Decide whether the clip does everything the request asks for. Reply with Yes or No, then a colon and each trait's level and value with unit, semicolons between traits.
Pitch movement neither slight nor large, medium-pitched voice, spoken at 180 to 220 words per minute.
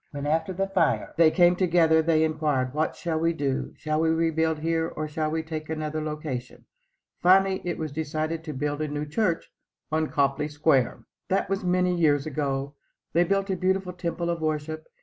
No: narrow, 2.1 semitones; medium, 160 Hz; average, 190 wpm